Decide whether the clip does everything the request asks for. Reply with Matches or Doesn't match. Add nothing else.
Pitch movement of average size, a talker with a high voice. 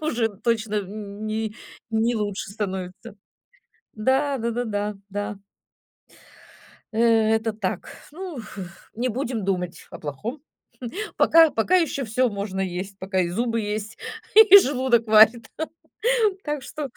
Matches